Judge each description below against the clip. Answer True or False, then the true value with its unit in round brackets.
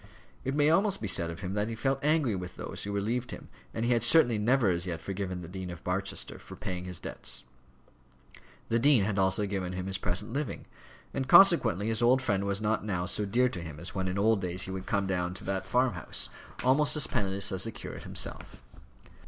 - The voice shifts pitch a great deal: False (4.7 semitones)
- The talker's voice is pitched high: False (100 Hz)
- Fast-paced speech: True (225 wpm)